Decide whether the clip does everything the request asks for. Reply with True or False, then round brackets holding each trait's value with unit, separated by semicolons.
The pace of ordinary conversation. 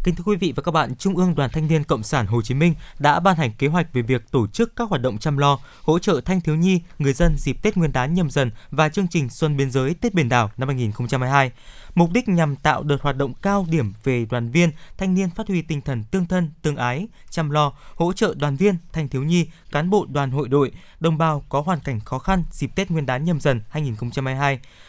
False (255 wpm)